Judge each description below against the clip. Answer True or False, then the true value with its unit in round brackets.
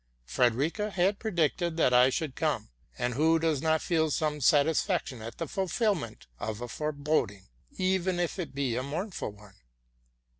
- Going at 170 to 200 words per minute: False (160 wpm)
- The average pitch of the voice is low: False (155 Hz)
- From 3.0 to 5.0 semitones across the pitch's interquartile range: False (5.6 semitones)